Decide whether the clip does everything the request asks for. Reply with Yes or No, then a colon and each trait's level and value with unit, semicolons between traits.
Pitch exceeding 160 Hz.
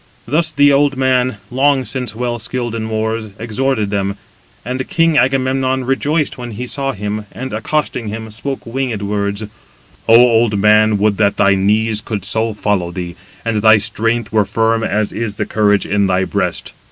No: low, 115 Hz